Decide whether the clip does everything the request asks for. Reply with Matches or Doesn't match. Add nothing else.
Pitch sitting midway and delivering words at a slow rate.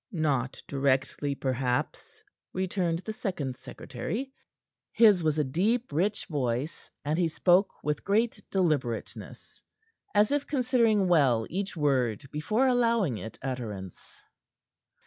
Matches